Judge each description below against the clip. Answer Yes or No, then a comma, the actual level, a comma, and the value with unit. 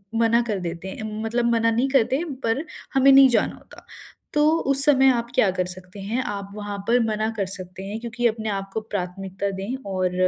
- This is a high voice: Yes, high, 215 Hz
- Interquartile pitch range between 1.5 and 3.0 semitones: No, average, 3.5 semitones